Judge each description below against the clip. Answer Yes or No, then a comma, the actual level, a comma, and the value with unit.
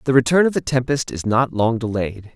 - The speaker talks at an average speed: No, fast, 230 wpm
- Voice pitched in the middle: No, low, 120 Hz